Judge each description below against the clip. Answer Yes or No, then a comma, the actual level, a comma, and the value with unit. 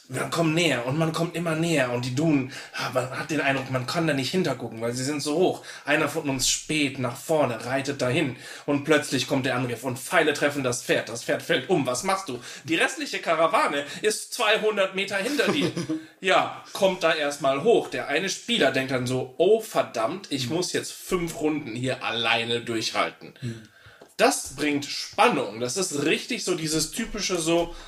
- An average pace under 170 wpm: No, fast, 190 wpm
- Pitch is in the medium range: Yes, medium, 145 Hz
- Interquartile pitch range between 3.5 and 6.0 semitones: Yes, average, 4.6 semitones